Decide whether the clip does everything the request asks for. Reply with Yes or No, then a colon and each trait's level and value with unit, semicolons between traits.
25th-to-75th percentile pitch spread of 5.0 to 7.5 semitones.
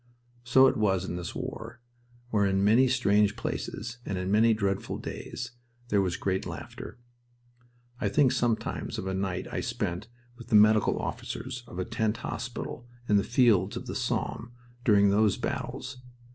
No: average, 3.6 semitones